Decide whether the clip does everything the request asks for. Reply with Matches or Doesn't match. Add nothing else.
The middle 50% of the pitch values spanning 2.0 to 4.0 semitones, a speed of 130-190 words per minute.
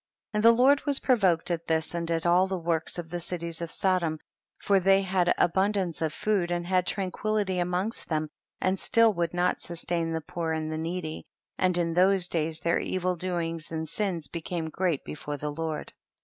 Doesn't match